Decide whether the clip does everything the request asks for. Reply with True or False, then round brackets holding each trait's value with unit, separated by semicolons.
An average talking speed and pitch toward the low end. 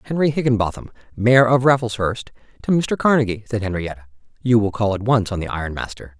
True (185 wpm; 115 Hz)